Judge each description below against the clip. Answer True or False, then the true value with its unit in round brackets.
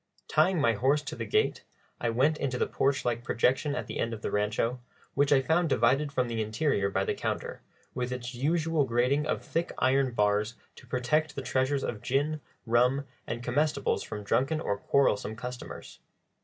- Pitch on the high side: False (130 Hz)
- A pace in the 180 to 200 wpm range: True (185 wpm)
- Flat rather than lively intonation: False (3.7 semitones)